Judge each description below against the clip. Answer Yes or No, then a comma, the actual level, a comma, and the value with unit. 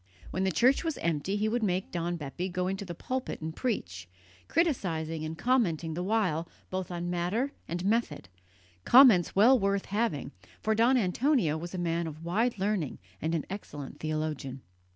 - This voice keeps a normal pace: Yes, average, 170 wpm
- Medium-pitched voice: Yes, medium, 180 Hz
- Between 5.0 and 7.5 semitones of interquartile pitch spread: Yes, average, 5.3 semitones